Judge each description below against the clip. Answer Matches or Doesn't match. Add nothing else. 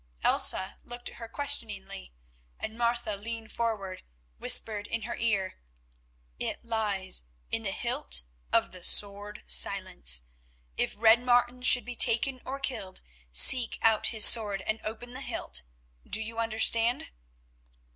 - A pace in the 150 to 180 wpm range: Doesn't match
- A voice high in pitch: Matches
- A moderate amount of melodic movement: Matches